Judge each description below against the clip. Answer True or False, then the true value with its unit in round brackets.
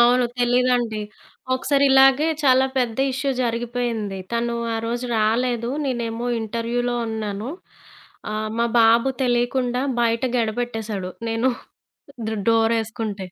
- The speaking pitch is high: True (235 Hz)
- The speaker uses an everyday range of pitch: False (1.7 semitones)